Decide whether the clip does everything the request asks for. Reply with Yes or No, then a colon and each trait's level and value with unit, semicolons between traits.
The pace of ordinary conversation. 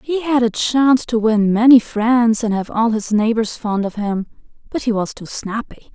No: fast, 210 wpm